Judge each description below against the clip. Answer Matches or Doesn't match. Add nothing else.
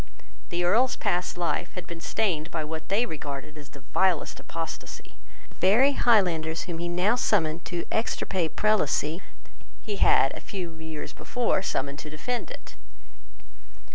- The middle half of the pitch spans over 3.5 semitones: Matches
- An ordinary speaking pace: Matches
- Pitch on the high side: Doesn't match